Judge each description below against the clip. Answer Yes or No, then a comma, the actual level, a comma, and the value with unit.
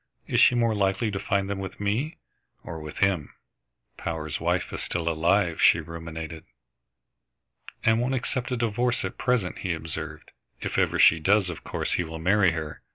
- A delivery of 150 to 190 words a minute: Yes, average, 175 wpm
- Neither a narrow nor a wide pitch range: Yes, average, 4.8 semitones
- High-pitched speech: No, very low, 95 Hz